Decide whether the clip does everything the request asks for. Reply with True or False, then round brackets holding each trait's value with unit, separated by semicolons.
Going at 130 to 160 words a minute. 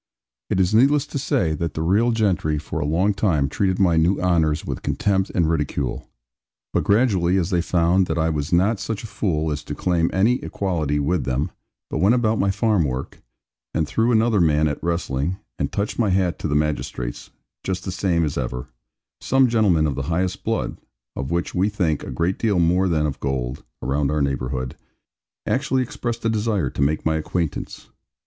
False (195 wpm)